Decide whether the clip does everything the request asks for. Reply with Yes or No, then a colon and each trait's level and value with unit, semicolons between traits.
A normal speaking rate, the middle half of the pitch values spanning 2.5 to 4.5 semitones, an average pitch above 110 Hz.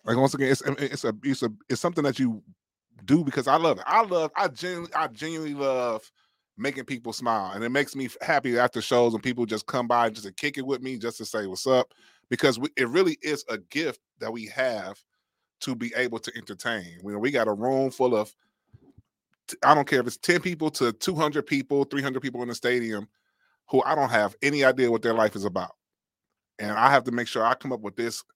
No: fast, 235 wpm; average, 3.4 semitones; low, 125 Hz